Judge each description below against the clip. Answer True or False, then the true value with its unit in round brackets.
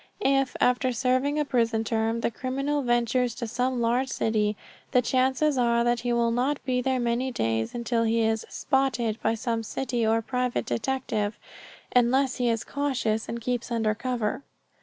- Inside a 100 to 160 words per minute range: False (170 wpm)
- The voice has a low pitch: False (240 Hz)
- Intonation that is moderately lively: False (2.2 semitones)